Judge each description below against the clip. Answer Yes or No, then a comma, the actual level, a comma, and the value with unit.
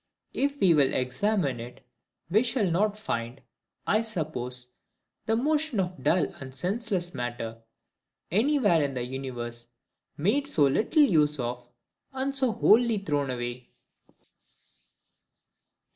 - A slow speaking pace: Yes, slow, 125 wpm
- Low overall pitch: No, medium, 170 Hz